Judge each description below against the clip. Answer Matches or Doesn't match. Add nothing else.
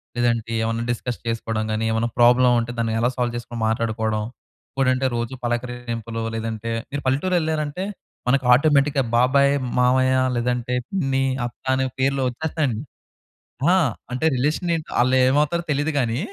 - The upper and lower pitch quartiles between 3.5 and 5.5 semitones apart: Doesn't match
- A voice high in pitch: Doesn't match